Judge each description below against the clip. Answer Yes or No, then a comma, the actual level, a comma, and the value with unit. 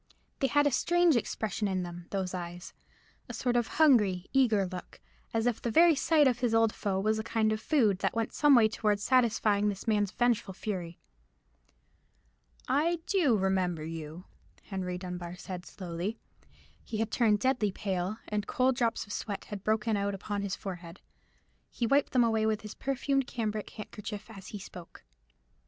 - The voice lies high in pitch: Yes, high, 215 Hz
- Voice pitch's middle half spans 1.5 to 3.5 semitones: No, average, 4.0 semitones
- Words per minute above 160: Yes, average, 175 wpm